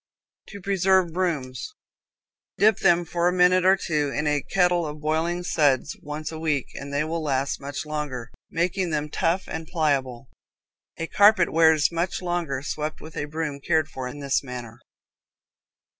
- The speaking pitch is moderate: Yes, medium, 155 Hz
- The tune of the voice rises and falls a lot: No, average, 3.5 semitones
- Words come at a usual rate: Yes, average, 165 wpm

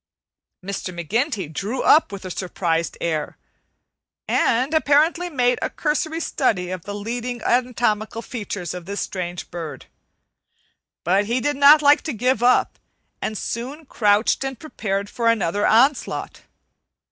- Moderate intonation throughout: No, wide, 5.7 semitones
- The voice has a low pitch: No, high, 230 Hz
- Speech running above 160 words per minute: No, slow, 135 wpm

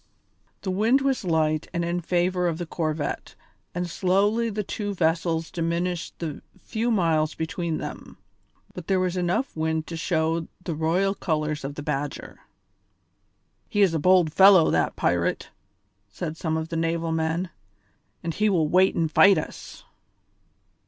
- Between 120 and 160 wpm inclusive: Yes, average, 155 wpm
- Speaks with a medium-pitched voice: Yes, medium, 170 Hz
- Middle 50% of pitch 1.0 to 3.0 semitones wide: Yes, narrow, 2.6 semitones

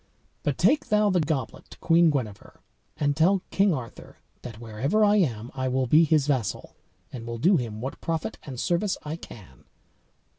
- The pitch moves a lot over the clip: Yes, wide, 6.3 semitones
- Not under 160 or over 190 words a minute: Yes, average, 180 wpm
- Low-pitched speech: No, medium, 145 Hz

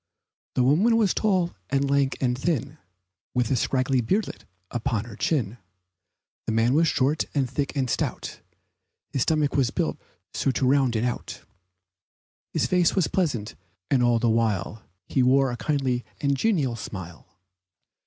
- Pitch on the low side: Yes, low, 130 Hz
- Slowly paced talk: No, average, 155 wpm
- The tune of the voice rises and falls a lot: No, average, 3.6 semitones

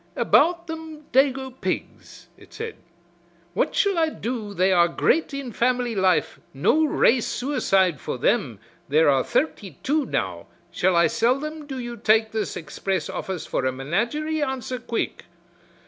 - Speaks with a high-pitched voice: Yes, high, 240 Hz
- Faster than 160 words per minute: No, average, 155 wpm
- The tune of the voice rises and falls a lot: Yes, wide, 7.7 semitones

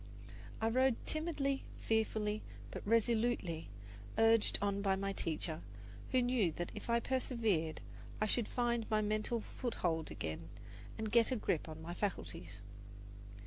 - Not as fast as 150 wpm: Yes, average, 140 wpm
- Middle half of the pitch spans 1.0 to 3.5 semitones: No, average, 4.8 semitones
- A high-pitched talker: Yes, high, 215 Hz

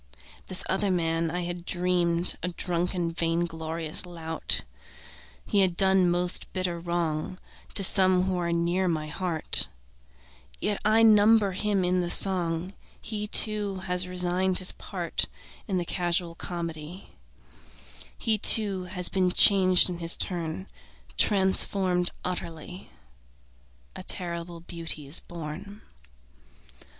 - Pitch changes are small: Yes, narrow, 2.0 semitones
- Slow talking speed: Yes, slow, 125 wpm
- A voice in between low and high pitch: Yes, medium, 180 Hz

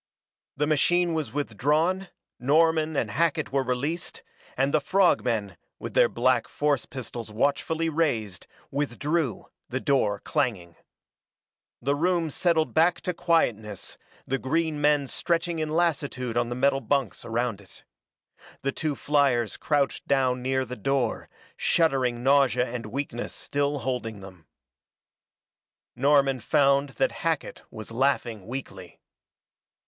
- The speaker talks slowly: Yes, slow, 130 wpm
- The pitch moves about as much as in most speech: Yes, average, 4.3 semitones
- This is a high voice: No, low, 135 Hz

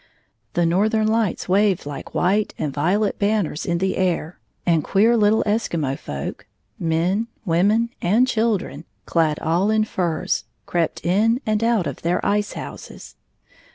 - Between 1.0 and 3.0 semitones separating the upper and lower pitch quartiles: No, average, 4.3 semitones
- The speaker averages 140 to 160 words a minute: Yes, average, 155 wpm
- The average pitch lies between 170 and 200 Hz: Yes, high, 190 Hz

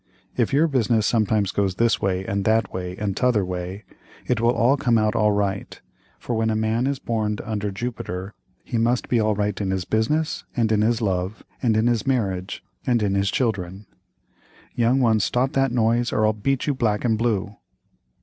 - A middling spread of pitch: Yes, average, 3.0 semitones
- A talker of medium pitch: No, low, 110 Hz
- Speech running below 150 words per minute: No, average, 195 wpm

